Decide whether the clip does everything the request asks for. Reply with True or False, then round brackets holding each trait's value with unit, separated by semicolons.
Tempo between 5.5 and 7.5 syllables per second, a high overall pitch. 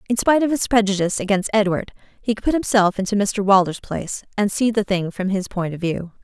True (6.2 syllables/s; 205 Hz)